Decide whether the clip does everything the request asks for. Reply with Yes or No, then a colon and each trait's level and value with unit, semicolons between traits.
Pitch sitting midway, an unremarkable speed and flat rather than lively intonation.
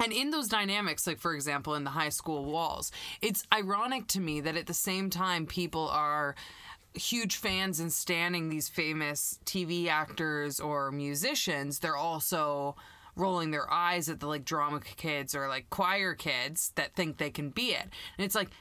No: medium, 165 Hz; average, 180 wpm; average, 4.0 semitones